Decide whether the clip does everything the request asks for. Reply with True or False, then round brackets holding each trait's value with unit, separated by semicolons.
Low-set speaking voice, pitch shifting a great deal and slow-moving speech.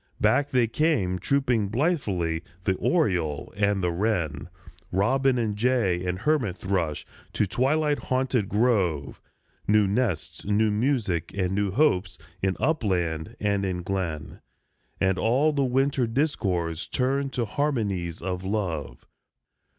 True (105 Hz; 6.1 semitones; 125 wpm)